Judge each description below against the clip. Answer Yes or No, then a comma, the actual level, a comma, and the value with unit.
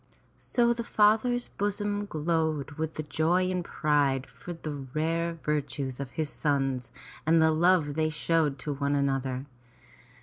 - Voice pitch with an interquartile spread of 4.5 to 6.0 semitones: No, average, 3.7 semitones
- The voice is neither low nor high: Yes, medium, 155 Hz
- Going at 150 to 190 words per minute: No, average, 140 wpm